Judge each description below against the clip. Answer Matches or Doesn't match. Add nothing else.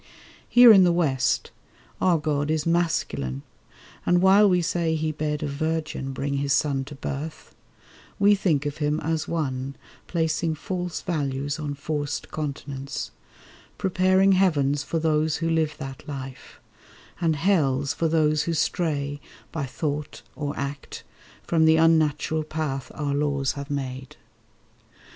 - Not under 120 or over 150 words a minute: Matches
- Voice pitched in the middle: Matches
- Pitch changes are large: Doesn't match